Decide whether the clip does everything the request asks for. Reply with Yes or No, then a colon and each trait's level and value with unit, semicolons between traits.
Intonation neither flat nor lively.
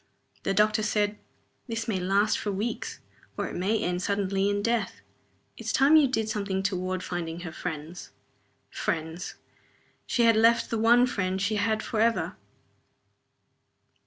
Yes: average, 3.3 semitones